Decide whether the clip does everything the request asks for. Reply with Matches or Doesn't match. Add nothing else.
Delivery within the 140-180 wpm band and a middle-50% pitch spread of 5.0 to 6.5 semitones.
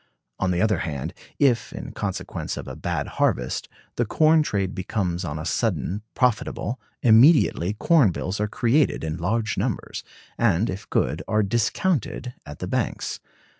Matches